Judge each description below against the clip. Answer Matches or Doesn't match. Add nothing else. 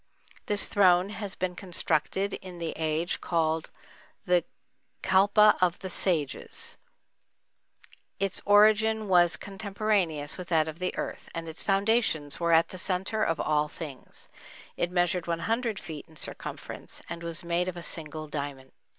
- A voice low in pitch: Doesn't match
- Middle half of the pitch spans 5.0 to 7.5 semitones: Doesn't match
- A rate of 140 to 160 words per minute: Matches